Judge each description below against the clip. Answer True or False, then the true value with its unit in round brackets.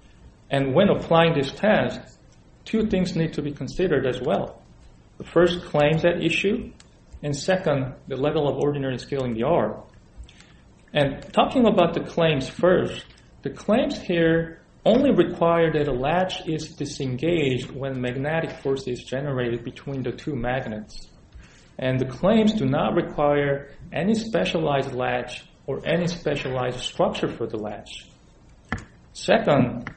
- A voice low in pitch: False (150 Hz)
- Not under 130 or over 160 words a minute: True (140 wpm)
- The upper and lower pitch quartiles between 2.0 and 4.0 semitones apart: False (4.8 semitones)